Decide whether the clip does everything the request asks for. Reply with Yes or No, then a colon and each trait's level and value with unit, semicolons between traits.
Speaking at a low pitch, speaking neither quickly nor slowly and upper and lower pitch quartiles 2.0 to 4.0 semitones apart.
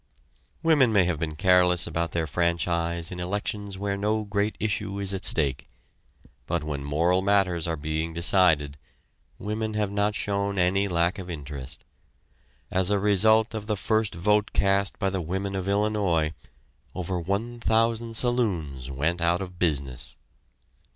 Yes: very low, 95 Hz; average, 150 wpm; average, 3.5 semitones